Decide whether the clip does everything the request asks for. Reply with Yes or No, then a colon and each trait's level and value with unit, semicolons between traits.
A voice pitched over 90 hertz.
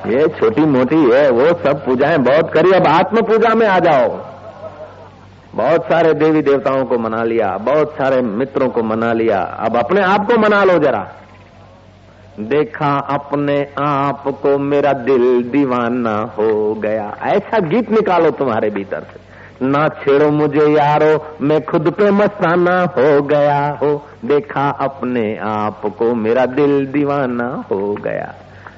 Yes: medium, 140 Hz